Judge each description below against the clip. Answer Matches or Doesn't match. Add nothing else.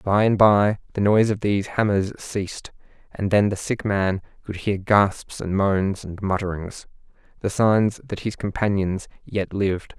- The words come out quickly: Doesn't match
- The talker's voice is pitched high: Doesn't match